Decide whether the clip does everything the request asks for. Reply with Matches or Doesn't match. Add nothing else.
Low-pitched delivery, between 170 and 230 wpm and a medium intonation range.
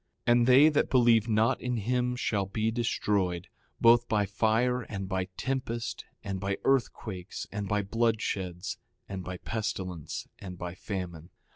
Doesn't match